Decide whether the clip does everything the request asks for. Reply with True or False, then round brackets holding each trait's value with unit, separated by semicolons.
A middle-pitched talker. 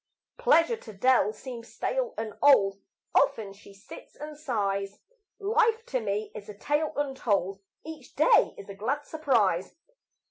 False (235 Hz)